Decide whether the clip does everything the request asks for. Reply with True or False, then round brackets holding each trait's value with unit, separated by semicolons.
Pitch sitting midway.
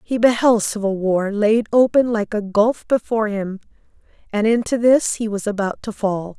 False (215 Hz)